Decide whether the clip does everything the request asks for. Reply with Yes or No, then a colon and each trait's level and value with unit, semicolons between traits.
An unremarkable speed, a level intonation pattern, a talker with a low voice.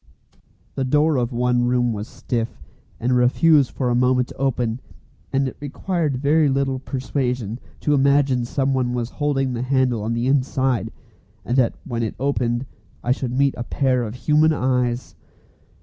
Yes: average, 165 wpm; narrow, 2.1 semitones; low, 130 Hz